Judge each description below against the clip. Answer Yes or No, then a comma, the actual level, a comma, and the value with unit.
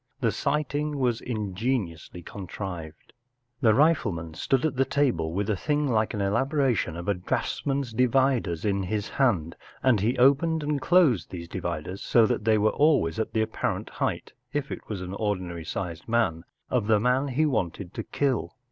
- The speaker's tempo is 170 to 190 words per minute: Yes, average, 175 wpm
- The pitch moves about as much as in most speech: No, wide, 6.6 semitones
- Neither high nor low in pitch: No, low, 110 Hz